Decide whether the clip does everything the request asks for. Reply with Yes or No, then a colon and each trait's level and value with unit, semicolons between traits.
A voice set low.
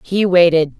No: medium, 175 Hz